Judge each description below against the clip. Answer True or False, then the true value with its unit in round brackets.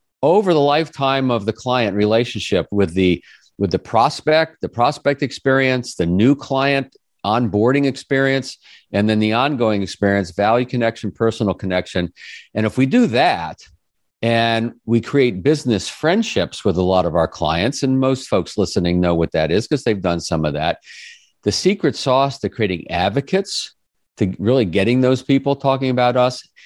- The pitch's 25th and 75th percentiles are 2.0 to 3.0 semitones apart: False (4.9 semitones)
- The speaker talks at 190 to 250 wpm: False (165 wpm)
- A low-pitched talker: True (120 Hz)